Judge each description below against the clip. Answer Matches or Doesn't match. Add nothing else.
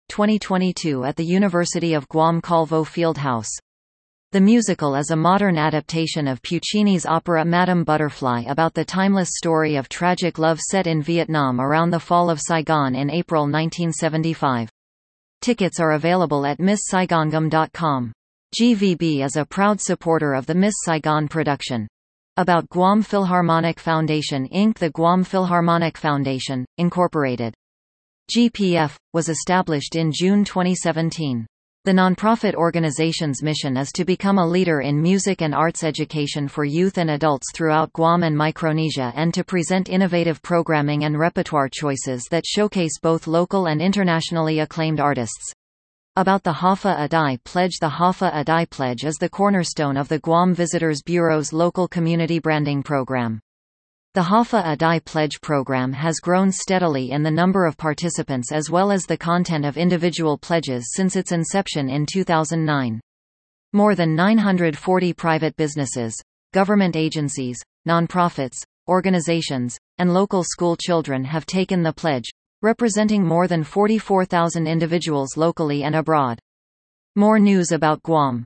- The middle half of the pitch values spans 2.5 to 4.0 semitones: Matches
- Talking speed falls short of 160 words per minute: Matches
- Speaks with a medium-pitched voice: Matches